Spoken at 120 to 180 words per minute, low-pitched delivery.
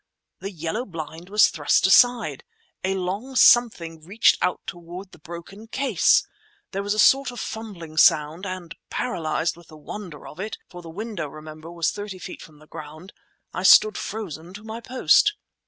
No: average, 165 wpm; medium, 185 Hz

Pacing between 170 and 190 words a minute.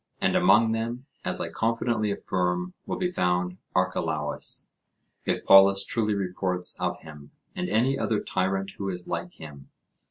No: average, 150 wpm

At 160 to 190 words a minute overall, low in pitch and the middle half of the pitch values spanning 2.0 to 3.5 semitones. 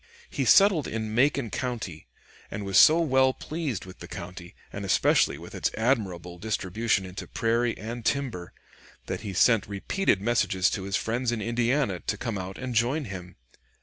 No: average, 170 wpm; low, 115 Hz; average, 4.8 semitones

